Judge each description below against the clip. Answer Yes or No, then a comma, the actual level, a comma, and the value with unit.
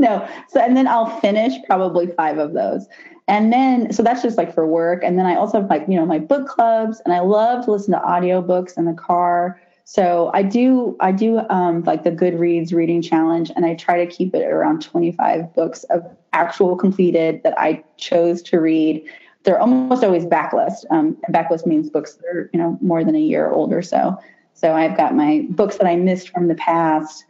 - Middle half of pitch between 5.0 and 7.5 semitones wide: Yes, average, 5.3 semitones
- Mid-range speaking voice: Yes, medium, 180 Hz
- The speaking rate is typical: No, fast, 215 wpm